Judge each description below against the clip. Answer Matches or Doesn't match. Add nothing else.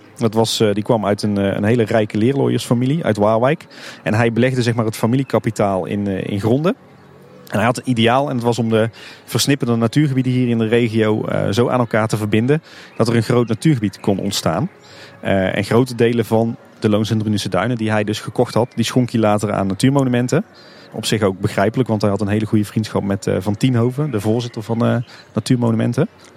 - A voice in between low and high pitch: Doesn't match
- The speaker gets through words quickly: Matches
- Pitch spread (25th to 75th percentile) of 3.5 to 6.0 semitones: Doesn't match